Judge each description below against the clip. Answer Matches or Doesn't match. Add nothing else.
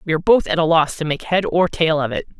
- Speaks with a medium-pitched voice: Matches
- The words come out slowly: Doesn't match